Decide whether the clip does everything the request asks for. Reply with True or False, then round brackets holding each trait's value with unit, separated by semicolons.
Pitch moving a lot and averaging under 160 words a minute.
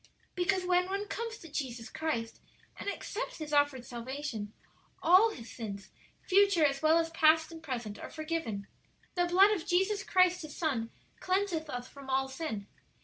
False (5.9 semitones; 165 wpm)